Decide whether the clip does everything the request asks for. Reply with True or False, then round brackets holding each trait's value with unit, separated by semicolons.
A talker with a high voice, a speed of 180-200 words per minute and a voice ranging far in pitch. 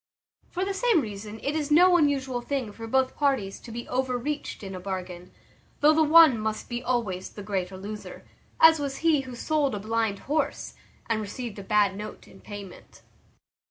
True (240 Hz; 185 wpm; 6.0 semitones)